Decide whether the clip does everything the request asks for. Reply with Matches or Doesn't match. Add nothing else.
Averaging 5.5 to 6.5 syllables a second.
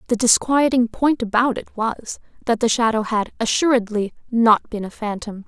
Doesn't match